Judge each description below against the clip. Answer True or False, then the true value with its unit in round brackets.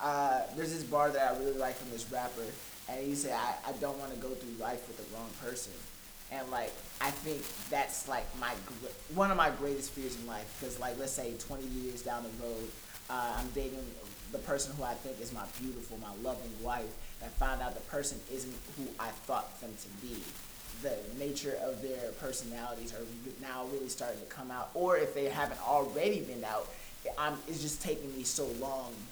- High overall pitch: False (130 Hz)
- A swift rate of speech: True (215 wpm)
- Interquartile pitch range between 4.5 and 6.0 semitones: False (2.8 semitones)